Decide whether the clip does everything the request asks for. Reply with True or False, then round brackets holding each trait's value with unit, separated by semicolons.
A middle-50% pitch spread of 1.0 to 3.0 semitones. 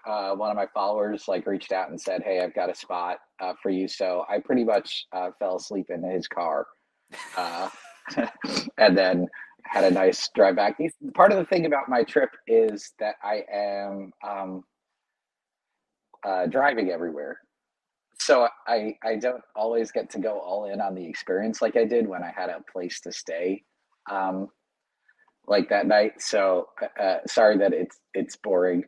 False (4.2 semitones)